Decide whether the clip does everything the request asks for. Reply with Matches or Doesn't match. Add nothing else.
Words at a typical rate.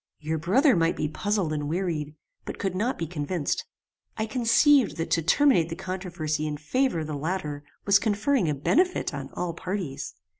Matches